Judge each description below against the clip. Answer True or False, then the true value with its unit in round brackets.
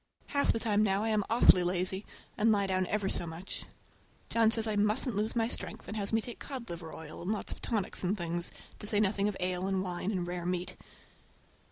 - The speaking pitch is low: False (200 Hz)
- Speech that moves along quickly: True (225 wpm)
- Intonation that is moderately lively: True (3.3 semitones)